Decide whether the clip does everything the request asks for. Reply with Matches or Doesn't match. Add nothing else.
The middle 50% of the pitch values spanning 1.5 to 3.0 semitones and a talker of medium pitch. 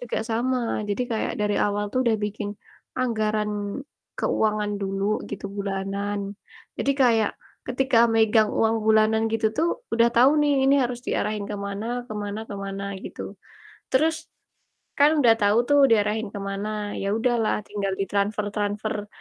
Doesn't match